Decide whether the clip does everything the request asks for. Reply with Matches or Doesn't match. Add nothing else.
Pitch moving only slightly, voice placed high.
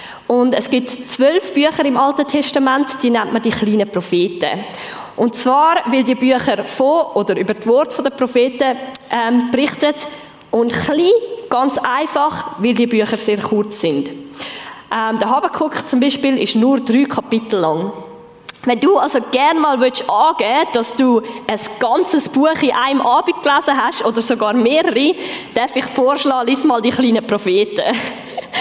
Doesn't match